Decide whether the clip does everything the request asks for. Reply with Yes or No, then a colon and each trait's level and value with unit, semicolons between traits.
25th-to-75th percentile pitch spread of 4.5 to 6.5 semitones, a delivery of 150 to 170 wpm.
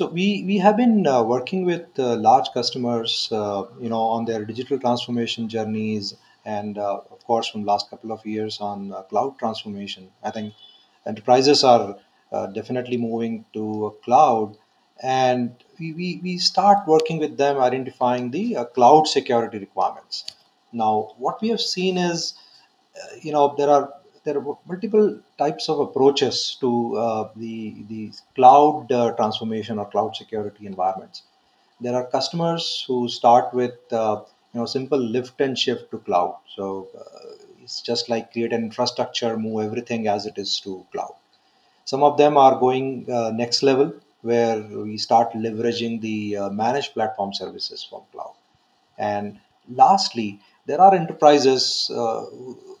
Yes: average, 5.0 semitones; average, 160 wpm